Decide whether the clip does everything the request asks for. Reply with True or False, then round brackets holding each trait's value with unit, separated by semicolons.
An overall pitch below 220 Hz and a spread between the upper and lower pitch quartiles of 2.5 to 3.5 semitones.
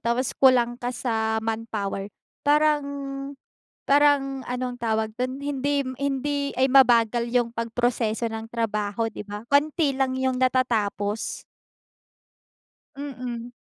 False (245 Hz; 3.2 semitones)